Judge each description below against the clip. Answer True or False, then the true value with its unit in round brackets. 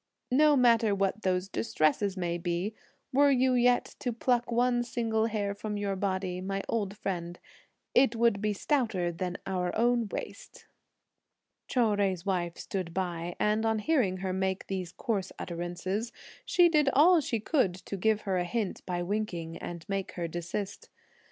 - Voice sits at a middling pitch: False (200 Hz)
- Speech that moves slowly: False (165 wpm)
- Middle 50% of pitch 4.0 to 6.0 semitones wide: True (4.3 semitones)